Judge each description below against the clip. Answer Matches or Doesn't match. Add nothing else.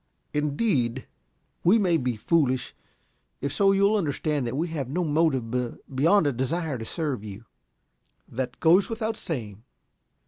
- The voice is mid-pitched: Matches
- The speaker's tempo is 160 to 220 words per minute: Doesn't match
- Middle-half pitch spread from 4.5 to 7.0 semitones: Matches